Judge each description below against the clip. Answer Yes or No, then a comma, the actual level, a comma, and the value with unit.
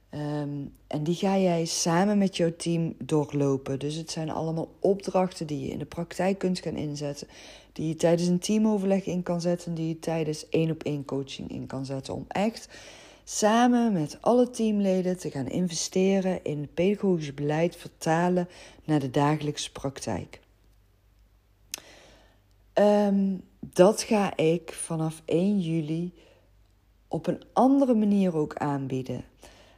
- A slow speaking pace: No, average, 145 wpm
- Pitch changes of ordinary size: Yes, average, 4.5 semitones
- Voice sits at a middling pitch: Yes, medium, 165 Hz